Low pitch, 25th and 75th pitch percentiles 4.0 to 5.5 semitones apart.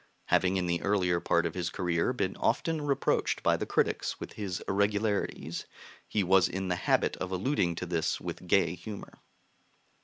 No: very low, 95 Hz; average, 2.7 semitones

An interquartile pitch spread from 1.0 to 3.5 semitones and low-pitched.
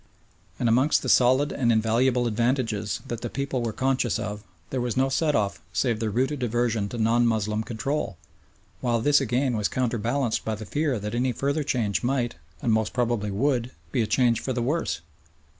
Yes: average, 3.1 semitones; low, 120 Hz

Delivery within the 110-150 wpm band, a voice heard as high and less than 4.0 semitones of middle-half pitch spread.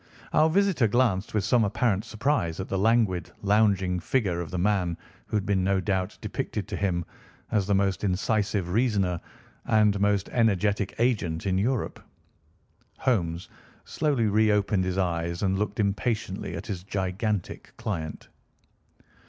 No: average, 145 wpm; low, 100 Hz; average, 2.8 semitones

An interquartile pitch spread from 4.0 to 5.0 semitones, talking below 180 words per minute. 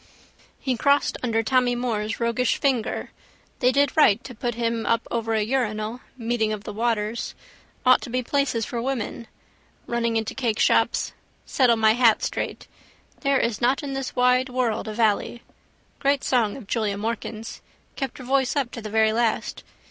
No: narrow, 2.4 semitones; average, 170 wpm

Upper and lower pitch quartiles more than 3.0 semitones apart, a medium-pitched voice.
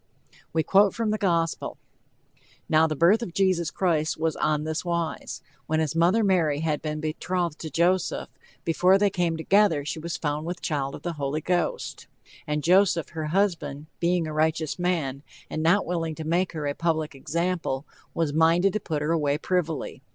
No: narrow, 2.6 semitones; medium, 165 Hz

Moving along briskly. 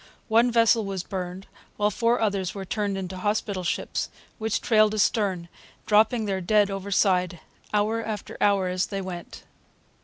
No: average, 150 wpm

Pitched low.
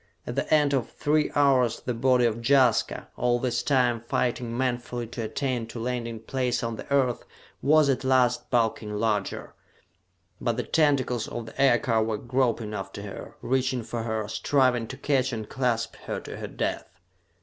Yes: low, 120 Hz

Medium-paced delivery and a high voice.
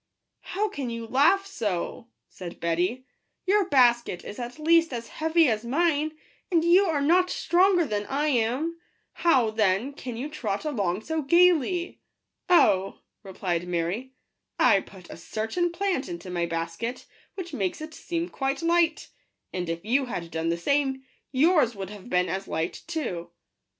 Yes: average, 175 wpm; very high, 255 Hz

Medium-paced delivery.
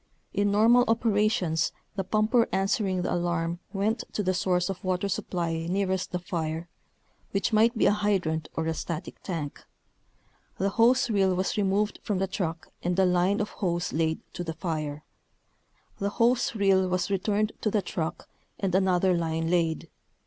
Yes: average, 170 wpm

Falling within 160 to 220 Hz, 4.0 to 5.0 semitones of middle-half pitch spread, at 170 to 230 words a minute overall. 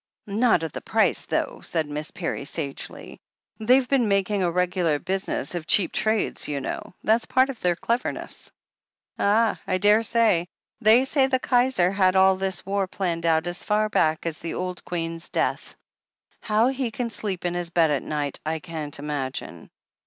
Yes: medium, 185 Hz; average, 4.7 semitones; average, 175 wpm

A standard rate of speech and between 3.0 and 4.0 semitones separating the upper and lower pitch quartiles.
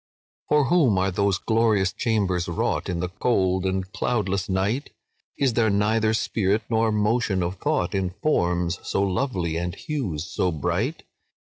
Yes: average, 150 wpm; average, 3.6 semitones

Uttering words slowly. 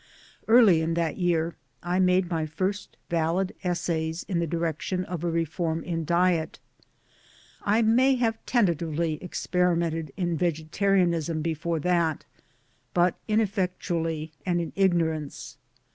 Yes: slow, 120 wpm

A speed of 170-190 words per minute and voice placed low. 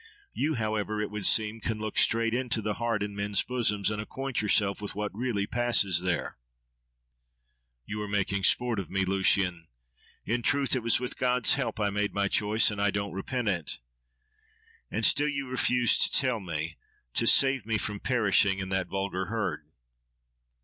Yes: average, 175 wpm; low, 105 Hz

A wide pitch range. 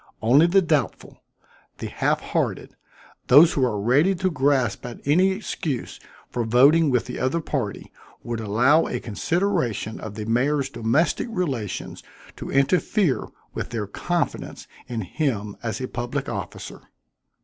Yes: wide, 6.0 semitones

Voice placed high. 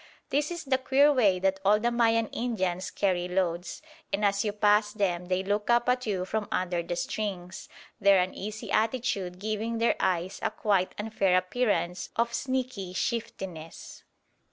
Yes: high, 205 Hz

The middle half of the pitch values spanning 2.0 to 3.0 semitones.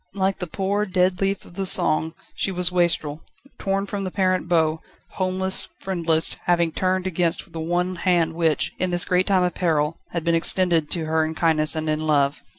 Yes: narrow, 2.5 semitones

